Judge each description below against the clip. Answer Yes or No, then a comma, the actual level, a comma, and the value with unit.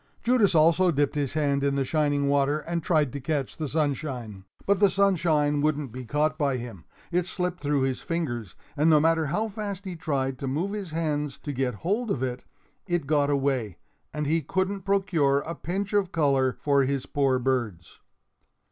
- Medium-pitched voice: Yes, medium, 150 Hz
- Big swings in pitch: No, average, 4.0 semitones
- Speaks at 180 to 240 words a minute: Yes, average, 190 wpm